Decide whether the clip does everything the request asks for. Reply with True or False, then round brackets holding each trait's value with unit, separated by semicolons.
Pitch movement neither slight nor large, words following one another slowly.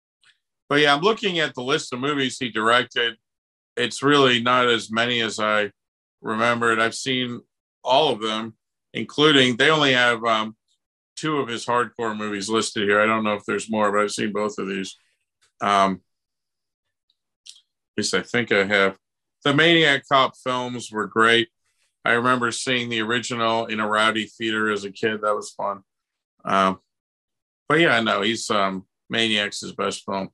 False (3.0 semitones; 170 wpm)